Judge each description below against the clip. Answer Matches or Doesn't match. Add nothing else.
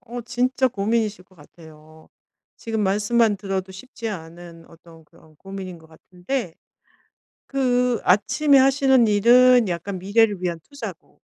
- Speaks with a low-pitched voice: Doesn't match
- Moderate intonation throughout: Doesn't match